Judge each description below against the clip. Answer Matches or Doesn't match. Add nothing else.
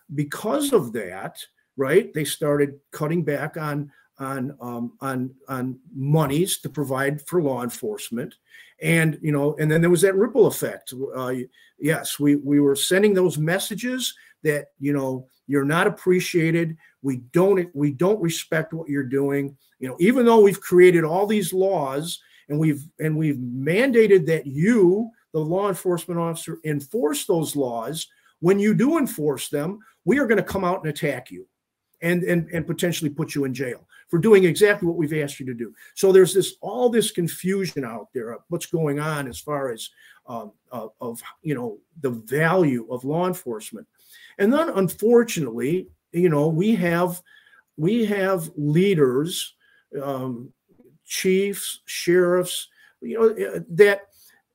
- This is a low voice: Doesn't match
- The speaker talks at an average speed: Matches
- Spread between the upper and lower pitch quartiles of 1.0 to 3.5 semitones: Doesn't match